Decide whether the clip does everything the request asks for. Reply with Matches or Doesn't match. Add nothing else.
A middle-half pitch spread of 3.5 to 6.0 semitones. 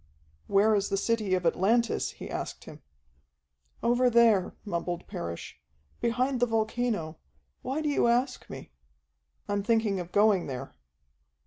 Matches